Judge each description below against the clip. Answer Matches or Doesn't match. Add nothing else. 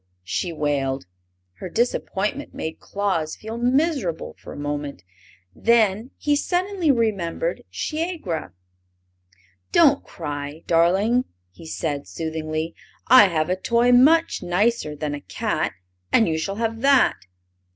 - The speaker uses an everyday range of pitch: Doesn't match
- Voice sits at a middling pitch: Doesn't match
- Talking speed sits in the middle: Doesn't match